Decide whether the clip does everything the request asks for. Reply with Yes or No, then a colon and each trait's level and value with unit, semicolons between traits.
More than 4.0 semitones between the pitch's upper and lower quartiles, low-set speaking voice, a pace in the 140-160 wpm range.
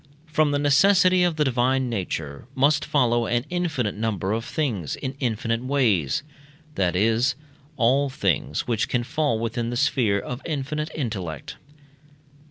Yes: average, 4.7 semitones; low, 125 Hz; average, 145 wpm